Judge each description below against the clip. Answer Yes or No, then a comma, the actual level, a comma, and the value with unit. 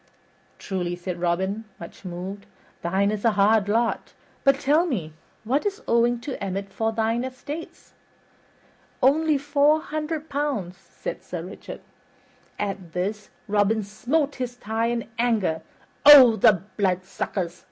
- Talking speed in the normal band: No, slow, 130 wpm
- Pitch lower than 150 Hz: No, high, 220 Hz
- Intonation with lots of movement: Yes, wide, 6.0 semitones